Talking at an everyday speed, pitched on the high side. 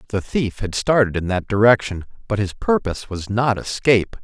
No: average, 185 wpm; low, 105 Hz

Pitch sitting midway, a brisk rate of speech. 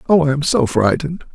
Yes: medium, 150 Hz; fast, 225 wpm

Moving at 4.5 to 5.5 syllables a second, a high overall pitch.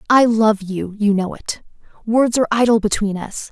Yes: 5.0 syllables/s; high, 215 Hz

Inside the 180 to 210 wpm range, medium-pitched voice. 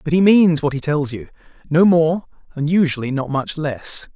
Yes: average, 200 wpm; medium, 155 Hz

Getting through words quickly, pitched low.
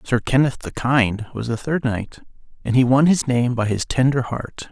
Yes: fast, 215 wpm; low, 125 Hz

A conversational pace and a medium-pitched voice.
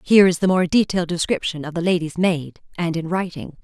No: fast, 215 wpm; medium, 170 Hz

